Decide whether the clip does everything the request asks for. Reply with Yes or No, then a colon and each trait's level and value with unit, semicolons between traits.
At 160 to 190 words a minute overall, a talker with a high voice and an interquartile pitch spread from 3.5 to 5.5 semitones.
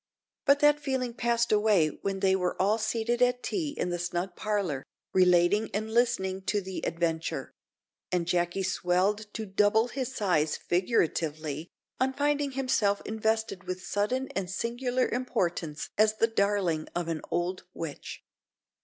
No: average, 145 wpm; high, 205 Hz; average, 5.0 semitones